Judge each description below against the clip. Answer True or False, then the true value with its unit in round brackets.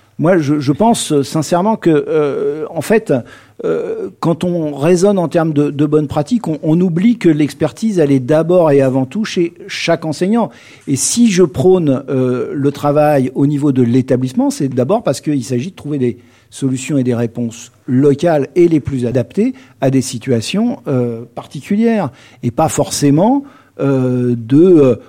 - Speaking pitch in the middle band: True (150 Hz)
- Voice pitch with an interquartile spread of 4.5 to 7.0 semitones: True (5.2 semitones)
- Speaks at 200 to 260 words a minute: False (170 wpm)